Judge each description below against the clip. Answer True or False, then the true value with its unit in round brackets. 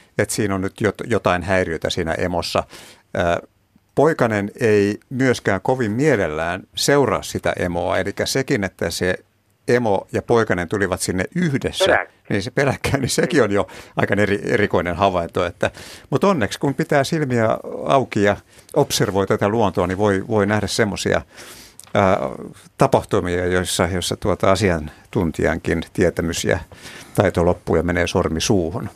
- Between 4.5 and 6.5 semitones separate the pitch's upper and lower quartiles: True (4.8 semitones)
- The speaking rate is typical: True (135 wpm)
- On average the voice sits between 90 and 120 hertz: True (100 Hz)